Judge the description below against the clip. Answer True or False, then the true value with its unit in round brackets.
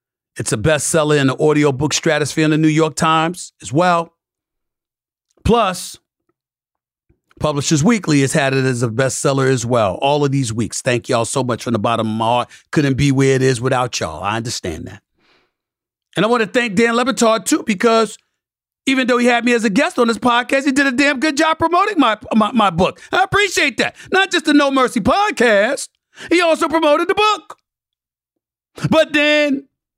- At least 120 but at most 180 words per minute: False (195 wpm)